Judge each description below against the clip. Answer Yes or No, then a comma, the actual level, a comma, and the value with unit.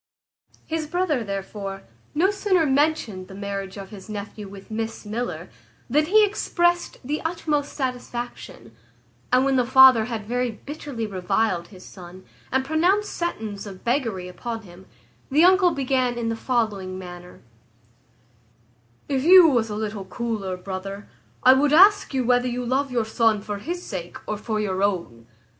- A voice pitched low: No, high, 230 Hz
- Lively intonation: Yes, wide, 6.2 semitones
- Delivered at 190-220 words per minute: No, average, 155 wpm